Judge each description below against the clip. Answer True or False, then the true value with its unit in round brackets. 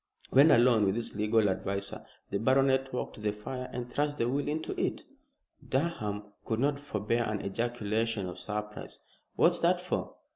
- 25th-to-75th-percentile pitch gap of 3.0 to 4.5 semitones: True (4.0 semitones)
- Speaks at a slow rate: False (170 wpm)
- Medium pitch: False (115 Hz)